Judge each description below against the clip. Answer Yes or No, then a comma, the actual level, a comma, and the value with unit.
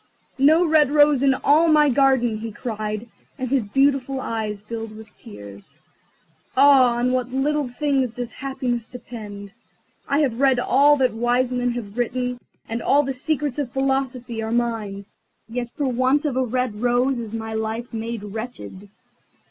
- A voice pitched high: Yes, high, 245 Hz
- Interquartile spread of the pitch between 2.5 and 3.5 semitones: Yes, average, 3.2 semitones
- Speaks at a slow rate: No, average, 165 wpm